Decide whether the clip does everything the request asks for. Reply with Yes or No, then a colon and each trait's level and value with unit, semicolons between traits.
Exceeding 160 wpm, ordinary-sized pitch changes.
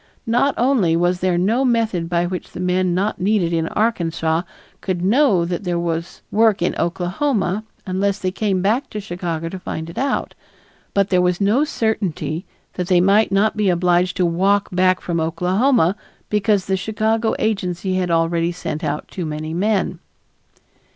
Yes: average, 170 wpm; average, 3.4 semitones